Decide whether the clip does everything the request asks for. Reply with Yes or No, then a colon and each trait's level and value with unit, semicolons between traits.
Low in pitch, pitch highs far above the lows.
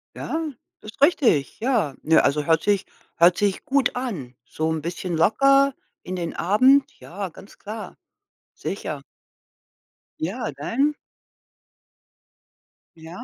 No: high, 195 Hz; wide, 8.0 semitones